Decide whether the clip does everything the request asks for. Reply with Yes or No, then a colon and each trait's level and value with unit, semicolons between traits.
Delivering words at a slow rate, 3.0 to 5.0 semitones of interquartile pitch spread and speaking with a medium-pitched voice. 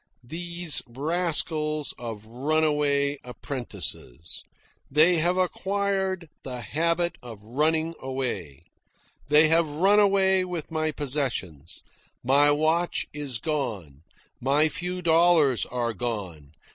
No: slow, 105 wpm; wide, 5.4 semitones; medium, 150 Hz